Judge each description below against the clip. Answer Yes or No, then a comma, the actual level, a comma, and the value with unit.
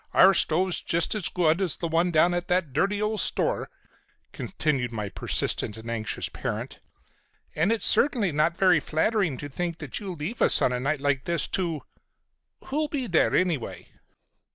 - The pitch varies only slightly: No, average, 4.6 semitones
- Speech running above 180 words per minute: No, average, 170 wpm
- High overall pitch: No, medium, 170 Hz